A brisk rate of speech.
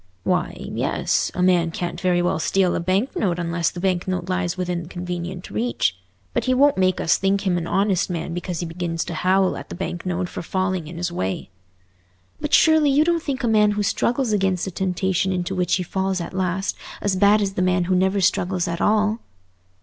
Yes: fast, 215 wpm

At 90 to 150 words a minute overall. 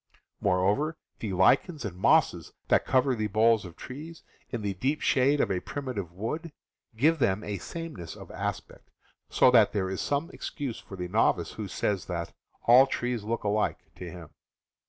No: average, 175 wpm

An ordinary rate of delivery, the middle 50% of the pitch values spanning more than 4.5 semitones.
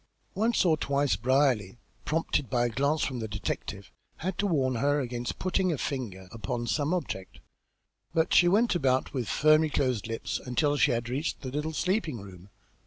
Yes: average, 175 wpm; average, 4.9 semitones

